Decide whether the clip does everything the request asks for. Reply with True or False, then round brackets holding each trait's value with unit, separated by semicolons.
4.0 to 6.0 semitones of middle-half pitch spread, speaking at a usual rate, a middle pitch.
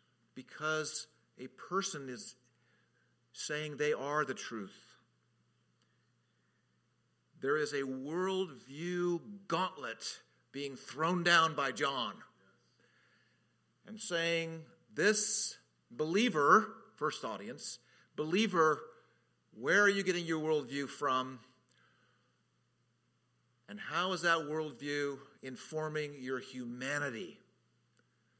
False (4.5 semitones; 85 wpm; 155 Hz)